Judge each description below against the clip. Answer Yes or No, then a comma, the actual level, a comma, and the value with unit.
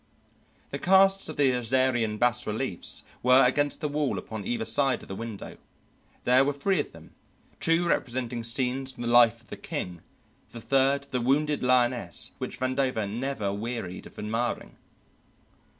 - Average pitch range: Yes, average, 3.0 semitones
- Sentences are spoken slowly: No, average, 160 wpm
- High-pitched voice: No, low, 125 Hz